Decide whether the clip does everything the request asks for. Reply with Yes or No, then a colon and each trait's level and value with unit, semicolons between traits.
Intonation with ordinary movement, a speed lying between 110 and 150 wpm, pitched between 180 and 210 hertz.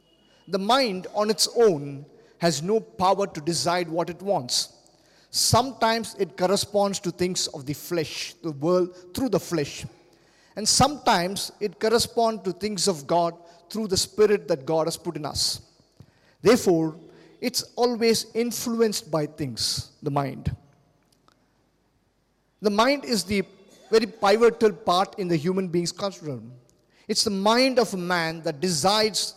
Yes: average, 4.6 semitones; average, 145 wpm; high, 190 Hz